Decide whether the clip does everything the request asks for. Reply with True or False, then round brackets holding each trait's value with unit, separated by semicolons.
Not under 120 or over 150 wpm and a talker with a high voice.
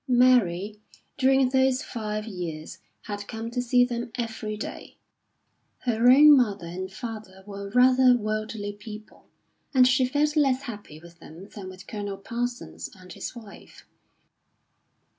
True (140 wpm; 220 Hz)